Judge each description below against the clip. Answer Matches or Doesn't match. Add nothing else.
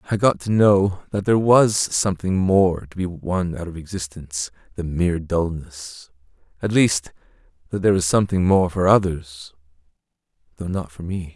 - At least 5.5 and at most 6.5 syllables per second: Doesn't match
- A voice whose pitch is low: Matches